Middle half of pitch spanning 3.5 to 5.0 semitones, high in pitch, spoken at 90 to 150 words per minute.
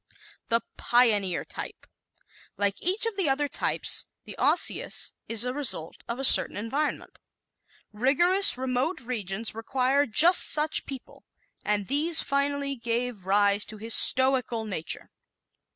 Yes: average, 4.7 semitones; very high, 250 Hz; slow, 135 wpm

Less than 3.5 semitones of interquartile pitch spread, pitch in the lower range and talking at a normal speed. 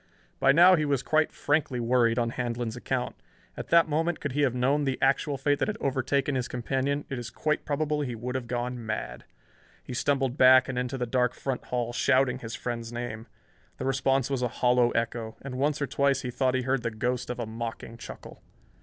No: narrow, 2.4 semitones; low, 130 Hz; fast, 215 wpm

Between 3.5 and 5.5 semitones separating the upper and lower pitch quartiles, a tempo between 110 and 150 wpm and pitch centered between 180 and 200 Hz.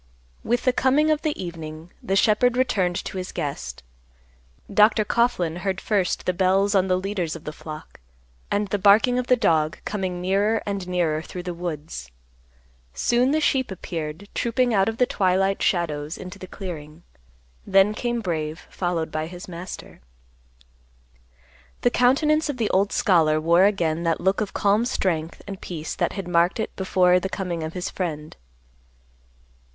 No: average, 3.9 semitones; average, 165 wpm; medium, 185 Hz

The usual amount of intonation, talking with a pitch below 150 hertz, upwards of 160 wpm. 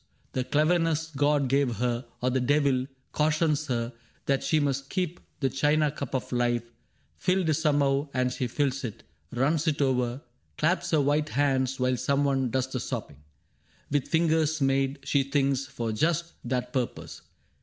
Yes: average, 3.0 semitones; low, 135 Hz; average, 175 wpm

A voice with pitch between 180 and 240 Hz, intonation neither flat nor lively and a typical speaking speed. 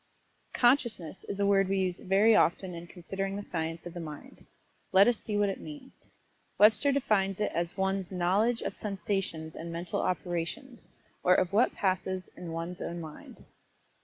Yes: high, 190 Hz; average, 3.1 semitones; average, 170 wpm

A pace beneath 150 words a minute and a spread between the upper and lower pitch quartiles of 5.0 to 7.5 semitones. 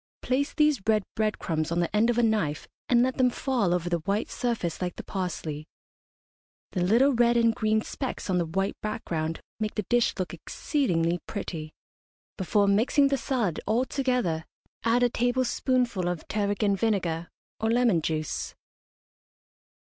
No: average, 160 wpm; wide, 5.6 semitones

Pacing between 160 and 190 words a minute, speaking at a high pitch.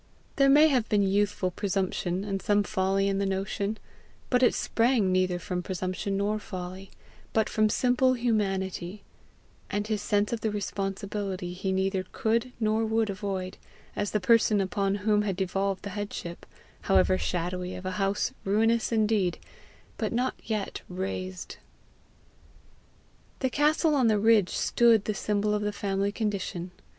No: average, 150 wpm; high, 200 Hz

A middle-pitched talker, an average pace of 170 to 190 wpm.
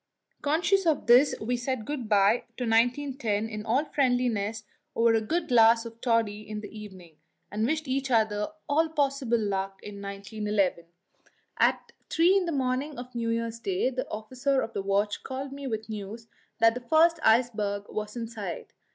No: high, 230 Hz; average, 175 wpm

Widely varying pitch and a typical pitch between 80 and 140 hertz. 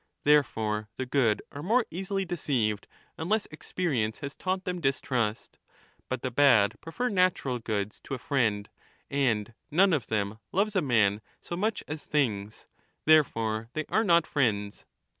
Yes: wide, 7.8 semitones; low, 135 Hz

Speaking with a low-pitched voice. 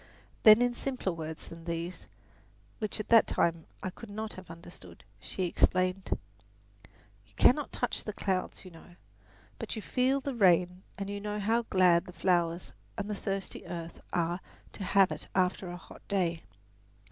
No: medium, 185 Hz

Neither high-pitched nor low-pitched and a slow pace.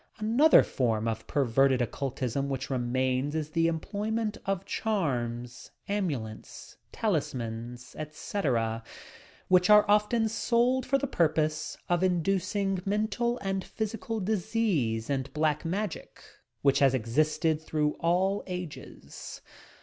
Yes: medium, 160 Hz; slow, 115 wpm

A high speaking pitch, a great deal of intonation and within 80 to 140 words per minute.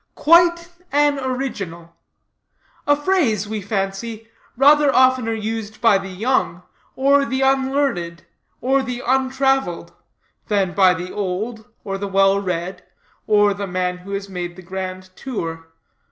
Yes: high, 210 Hz; wide, 6.0 semitones; slow, 135 wpm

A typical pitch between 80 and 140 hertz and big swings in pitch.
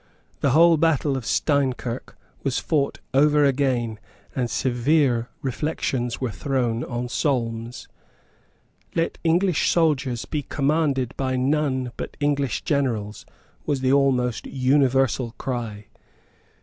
No: low, 135 Hz; average, 3.0 semitones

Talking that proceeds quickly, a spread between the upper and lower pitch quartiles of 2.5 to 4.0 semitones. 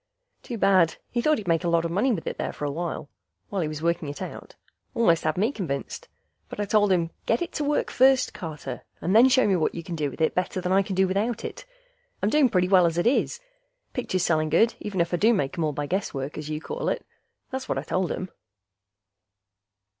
No: fast, 235 wpm; average, 5.0 semitones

